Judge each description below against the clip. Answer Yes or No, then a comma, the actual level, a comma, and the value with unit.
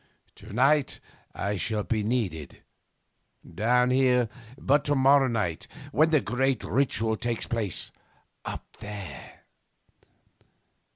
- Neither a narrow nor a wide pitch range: Yes, average, 4.2 semitones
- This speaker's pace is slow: Yes, slow, 110 wpm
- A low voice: Yes, low, 120 Hz